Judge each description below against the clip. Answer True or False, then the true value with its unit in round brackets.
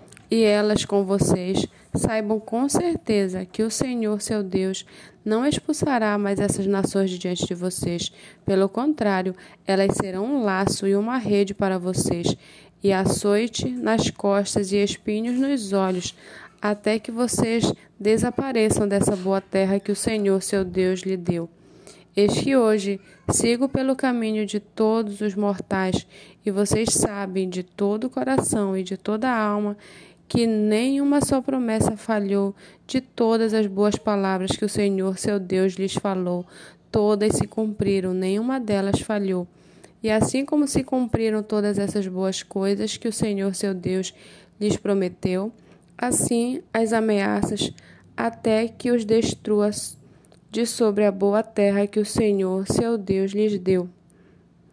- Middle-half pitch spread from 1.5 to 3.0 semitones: True (2.4 semitones)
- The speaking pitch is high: True (205 Hz)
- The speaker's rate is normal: True (145 wpm)